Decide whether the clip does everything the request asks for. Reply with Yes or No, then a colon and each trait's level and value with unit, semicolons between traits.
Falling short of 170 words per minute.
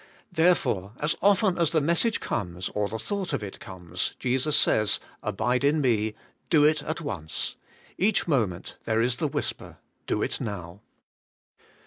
Yes: average, 155 wpm